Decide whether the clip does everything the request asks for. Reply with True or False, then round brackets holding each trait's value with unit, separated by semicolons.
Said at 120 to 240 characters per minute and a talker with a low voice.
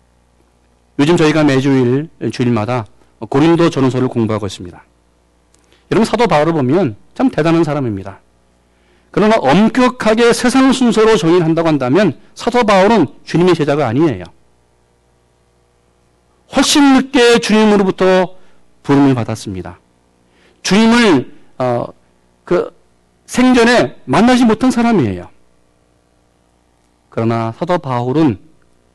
False (260 characters per minute; 120 Hz)